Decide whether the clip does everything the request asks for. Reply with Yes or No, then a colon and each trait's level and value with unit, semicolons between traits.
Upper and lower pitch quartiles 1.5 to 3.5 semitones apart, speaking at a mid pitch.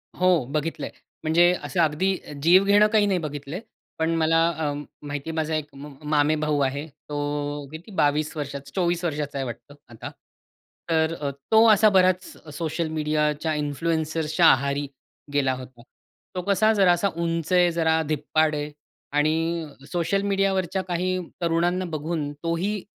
Yes: average, 3.2 semitones; medium, 160 Hz